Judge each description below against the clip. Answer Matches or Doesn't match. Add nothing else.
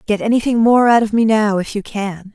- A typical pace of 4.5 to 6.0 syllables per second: Matches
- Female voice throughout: Matches